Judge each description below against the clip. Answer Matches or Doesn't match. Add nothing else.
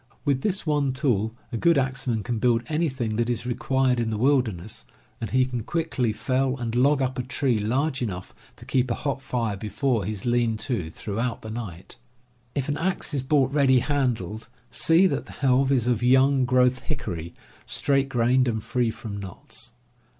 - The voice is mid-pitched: Doesn't match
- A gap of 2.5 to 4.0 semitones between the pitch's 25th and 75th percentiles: Matches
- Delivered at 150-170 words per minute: Doesn't match